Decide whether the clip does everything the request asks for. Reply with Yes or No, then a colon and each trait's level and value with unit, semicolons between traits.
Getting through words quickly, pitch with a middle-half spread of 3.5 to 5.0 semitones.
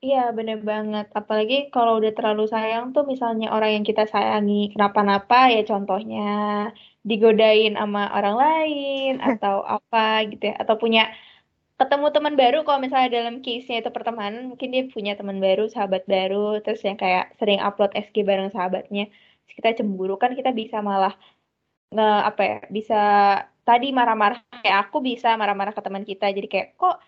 No: fast, 165 wpm; average, 2.8 semitones